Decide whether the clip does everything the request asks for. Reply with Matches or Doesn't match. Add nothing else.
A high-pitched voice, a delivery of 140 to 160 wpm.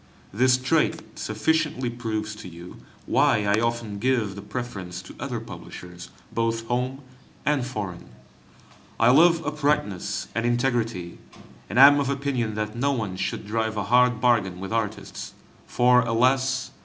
Doesn't match